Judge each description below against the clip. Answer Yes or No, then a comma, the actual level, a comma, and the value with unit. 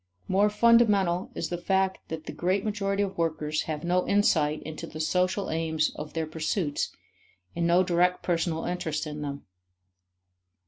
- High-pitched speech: No, medium, 175 Hz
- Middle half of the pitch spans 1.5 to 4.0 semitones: Yes, average, 3.4 semitones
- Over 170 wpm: No, average, 155 wpm